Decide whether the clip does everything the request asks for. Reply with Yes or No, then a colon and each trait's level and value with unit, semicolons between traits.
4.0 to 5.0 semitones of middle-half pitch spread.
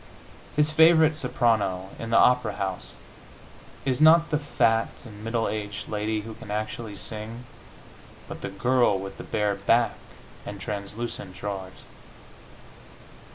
No: average, 3.4 semitones